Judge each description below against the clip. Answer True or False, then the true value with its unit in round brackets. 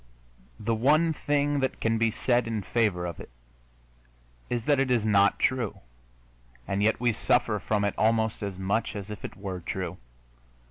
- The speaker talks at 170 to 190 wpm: True (175 wpm)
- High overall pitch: False (110 Hz)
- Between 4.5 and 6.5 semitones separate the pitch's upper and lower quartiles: False (3.4 semitones)